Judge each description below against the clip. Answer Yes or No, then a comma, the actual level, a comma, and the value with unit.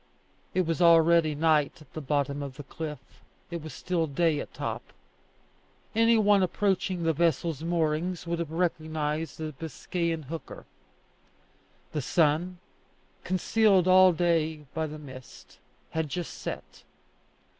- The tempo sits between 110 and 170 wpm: Yes, slow, 135 wpm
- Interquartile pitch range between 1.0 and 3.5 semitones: Yes, narrow, 2.4 semitones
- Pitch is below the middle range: No, medium, 165 Hz